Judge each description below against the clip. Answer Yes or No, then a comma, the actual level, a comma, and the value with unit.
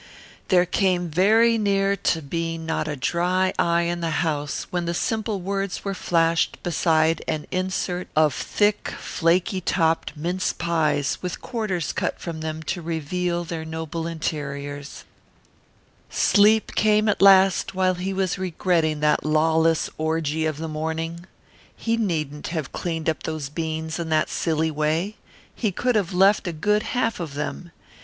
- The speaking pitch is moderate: Yes, medium, 170 Hz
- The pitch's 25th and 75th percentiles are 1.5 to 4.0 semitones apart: Yes, average, 3.0 semitones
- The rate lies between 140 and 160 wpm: Yes, average, 155 wpm